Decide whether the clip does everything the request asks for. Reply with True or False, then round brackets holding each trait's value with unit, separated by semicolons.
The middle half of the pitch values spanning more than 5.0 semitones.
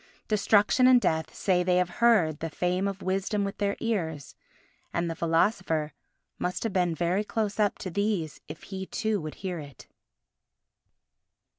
False (3.8 semitones)